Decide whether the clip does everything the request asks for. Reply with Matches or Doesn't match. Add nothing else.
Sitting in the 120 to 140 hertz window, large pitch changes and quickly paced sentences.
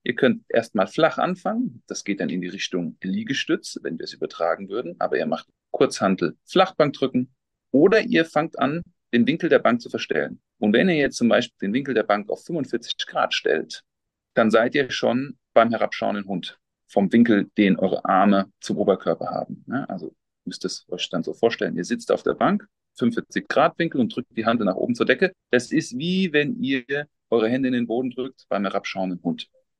Matches